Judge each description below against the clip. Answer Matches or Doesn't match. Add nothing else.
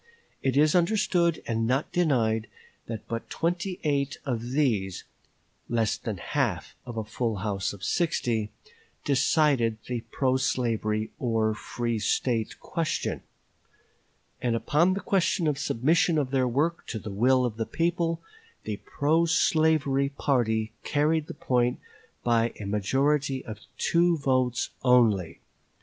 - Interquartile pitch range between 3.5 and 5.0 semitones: Doesn't match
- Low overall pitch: Matches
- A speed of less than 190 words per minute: Matches